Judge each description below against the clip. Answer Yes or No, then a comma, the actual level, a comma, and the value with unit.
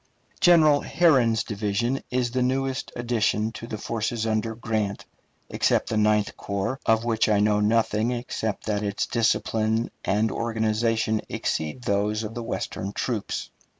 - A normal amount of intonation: No, narrow, 2.0 semitones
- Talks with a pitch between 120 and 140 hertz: No, low, 110 Hz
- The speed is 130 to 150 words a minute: Yes, average, 145 wpm